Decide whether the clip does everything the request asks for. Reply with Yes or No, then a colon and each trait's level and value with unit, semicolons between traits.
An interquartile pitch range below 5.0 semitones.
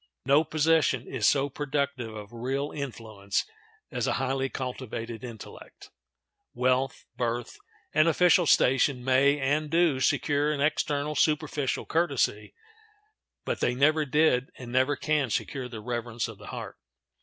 Yes: average, 3.3 semitones